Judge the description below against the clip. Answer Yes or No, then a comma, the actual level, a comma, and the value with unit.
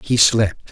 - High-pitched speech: No, low, 105 Hz